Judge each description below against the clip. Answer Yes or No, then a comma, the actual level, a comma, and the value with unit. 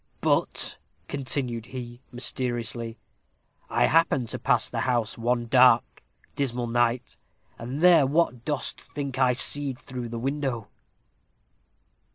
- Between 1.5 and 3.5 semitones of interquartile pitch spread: Yes, narrow, 2.4 semitones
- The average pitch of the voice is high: No, low, 125 Hz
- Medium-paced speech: No, slow, 120 wpm